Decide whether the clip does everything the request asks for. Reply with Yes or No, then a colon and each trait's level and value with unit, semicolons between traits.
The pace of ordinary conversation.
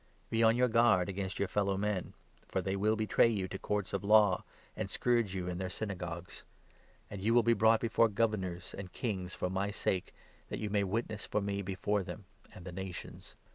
No: fast, 215 wpm